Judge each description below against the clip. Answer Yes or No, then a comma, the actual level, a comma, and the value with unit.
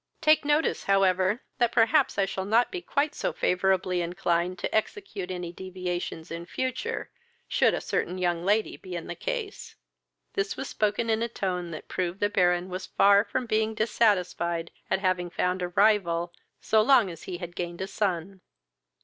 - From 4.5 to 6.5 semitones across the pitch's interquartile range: No, average, 3.7 semitones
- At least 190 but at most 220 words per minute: No, average, 175 wpm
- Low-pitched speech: No, high, 190 Hz